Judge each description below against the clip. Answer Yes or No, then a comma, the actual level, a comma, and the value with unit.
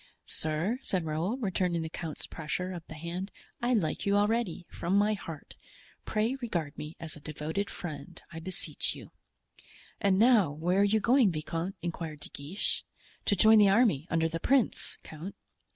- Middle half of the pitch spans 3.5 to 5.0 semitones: Yes, average, 4.4 semitones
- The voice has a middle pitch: Yes, medium, 180 Hz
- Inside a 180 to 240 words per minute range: No, average, 170 wpm